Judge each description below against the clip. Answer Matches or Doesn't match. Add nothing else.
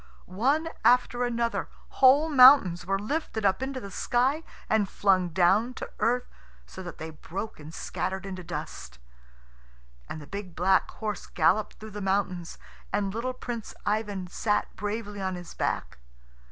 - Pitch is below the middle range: Doesn't match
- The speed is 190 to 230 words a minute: Doesn't match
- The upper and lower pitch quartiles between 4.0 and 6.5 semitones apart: Matches